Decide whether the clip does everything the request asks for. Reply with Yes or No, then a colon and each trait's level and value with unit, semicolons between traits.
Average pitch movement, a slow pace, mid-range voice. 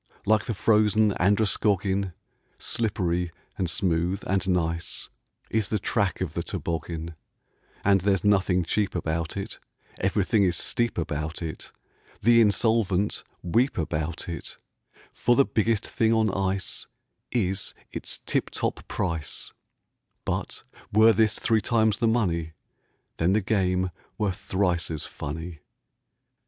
No: average, 4.0 semitones; slow, 125 wpm; very low, 95 Hz